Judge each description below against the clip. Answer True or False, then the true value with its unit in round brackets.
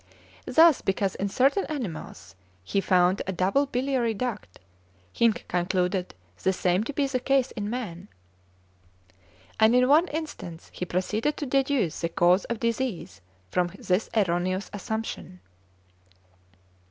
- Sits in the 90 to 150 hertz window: False (210 Hz)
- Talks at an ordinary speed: False (130 wpm)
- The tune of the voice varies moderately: False (5.9 semitones)